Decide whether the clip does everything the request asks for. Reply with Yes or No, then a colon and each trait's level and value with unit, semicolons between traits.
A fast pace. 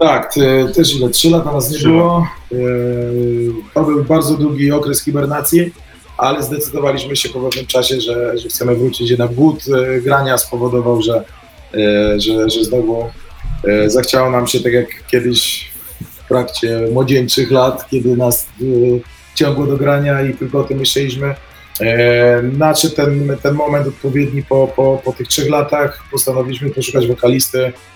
No: average, 150 wpm